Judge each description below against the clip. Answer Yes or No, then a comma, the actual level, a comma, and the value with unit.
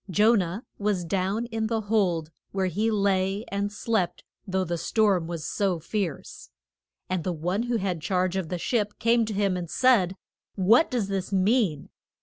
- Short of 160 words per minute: No, average, 175 wpm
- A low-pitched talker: No, high, 195 Hz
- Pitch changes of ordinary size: Yes, average, 3.1 semitones